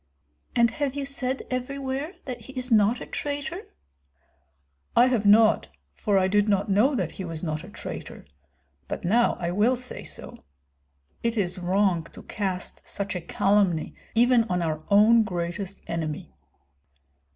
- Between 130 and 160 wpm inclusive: Yes, average, 155 wpm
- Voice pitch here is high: Yes, high, 210 Hz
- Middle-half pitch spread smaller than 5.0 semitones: No, wide, 5.5 semitones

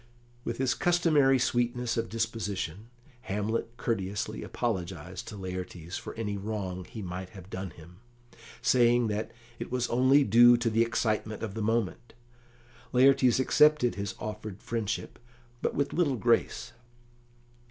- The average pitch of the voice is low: Yes, low, 115 Hz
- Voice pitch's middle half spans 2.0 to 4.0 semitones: Yes, average, 3.7 semitones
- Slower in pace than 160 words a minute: Yes, slow, 135 wpm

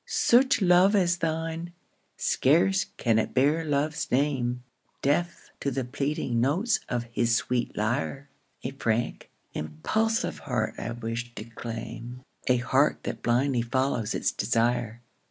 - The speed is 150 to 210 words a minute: No, slow, 135 wpm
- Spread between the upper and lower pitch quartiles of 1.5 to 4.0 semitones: No, average, 5.2 semitones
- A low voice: Yes, low, 130 Hz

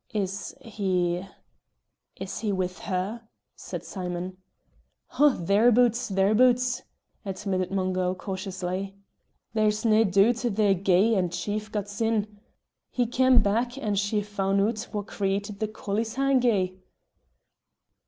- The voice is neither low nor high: No, high, 205 Hz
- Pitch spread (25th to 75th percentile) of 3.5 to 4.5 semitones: No, average, 2.9 semitones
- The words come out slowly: Yes, slow, 115 wpm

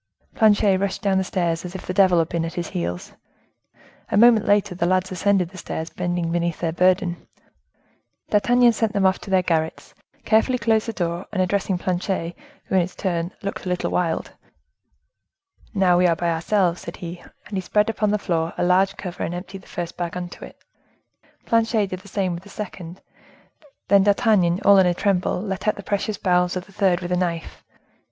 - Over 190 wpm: Yes, fast, 205 wpm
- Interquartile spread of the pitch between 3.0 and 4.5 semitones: No, narrow, 2.6 semitones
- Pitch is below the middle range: No, medium, 185 Hz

